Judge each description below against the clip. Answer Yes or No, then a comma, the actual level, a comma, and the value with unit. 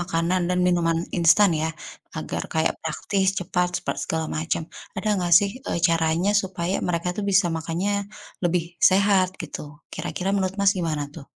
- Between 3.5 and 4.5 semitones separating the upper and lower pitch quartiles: No, narrow, 2.5 semitones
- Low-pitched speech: No, medium, 175 Hz